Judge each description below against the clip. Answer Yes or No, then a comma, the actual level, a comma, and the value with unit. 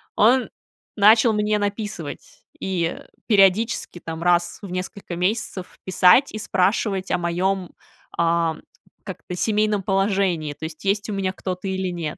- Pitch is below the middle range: No, high, 190 Hz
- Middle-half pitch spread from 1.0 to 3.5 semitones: Yes, average, 2.9 semitones